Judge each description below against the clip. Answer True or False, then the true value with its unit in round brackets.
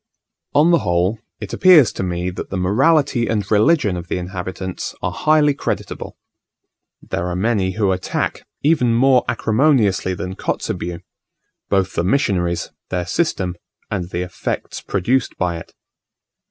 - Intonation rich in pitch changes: True (6.4 semitones)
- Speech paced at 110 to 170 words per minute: True (140 wpm)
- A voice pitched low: True (100 Hz)